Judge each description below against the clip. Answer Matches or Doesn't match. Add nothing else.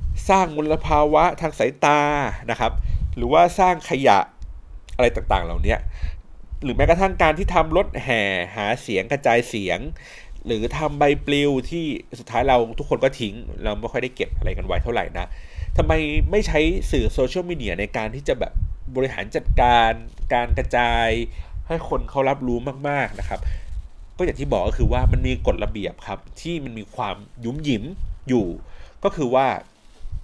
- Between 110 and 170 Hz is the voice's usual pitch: Matches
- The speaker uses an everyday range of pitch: Doesn't match